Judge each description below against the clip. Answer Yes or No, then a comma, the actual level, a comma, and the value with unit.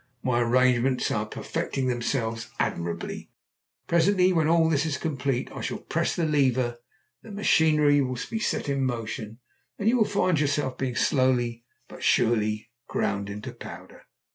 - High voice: No, low, 130 Hz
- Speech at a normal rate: Yes, average, 145 wpm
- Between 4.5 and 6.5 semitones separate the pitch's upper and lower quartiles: Yes, average, 4.8 semitones